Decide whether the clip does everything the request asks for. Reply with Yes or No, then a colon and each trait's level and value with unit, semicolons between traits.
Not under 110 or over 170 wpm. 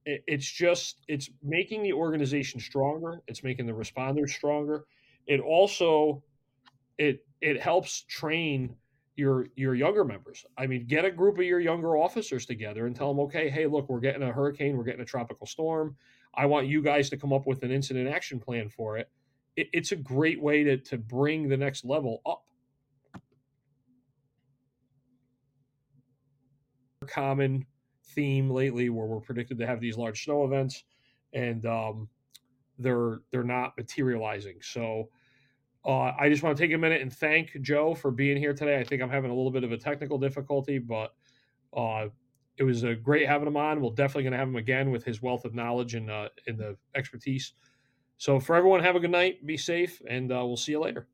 No: average, 185 wpm